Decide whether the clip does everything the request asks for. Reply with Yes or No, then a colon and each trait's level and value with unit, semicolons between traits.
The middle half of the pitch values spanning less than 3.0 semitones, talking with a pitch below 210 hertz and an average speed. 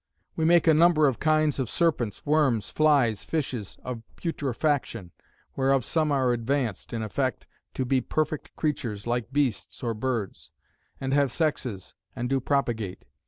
No: average, 4.5 semitones; low, 135 Hz; average, 150 wpm